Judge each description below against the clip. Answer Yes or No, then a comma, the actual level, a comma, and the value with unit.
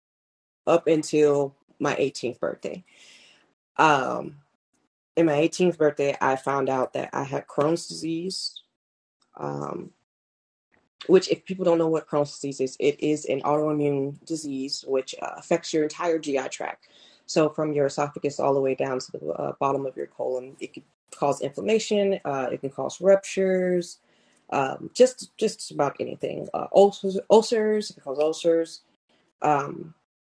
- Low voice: No, medium, 155 Hz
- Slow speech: No, average, 160 wpm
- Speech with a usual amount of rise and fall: Yes, average, 4.6 semitones